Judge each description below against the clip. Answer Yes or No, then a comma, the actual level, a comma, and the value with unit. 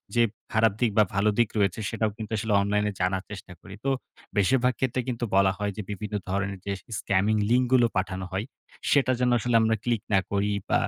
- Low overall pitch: Yes, low, 105 Hz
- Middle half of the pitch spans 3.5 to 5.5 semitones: No, average, 3.1 semitones